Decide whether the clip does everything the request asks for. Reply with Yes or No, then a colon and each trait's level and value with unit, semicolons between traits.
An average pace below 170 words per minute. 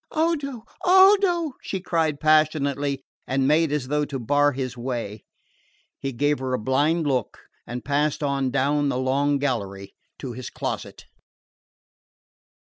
Yes: average, 140 wpm